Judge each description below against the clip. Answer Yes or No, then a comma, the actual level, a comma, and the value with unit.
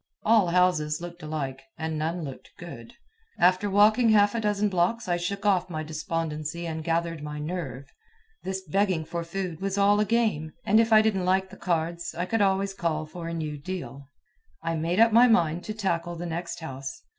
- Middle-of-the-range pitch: Yes, medium, 175 Hz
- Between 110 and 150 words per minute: No, average, 195 wpm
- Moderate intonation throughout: Yes, average, 3.9 semitones